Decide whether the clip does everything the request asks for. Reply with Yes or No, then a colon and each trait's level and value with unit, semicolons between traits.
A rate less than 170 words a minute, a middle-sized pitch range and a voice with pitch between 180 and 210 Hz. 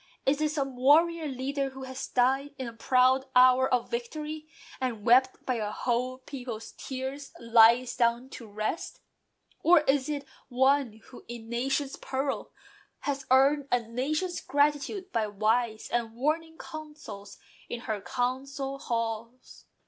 No: average, 145 wpm; average, 3.1 semitones; very high, 260 Hz